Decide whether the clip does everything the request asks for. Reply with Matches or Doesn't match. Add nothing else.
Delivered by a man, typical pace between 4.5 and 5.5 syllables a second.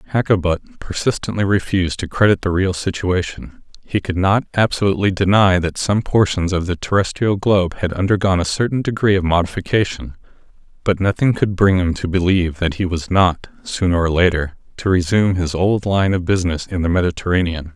Doesn't match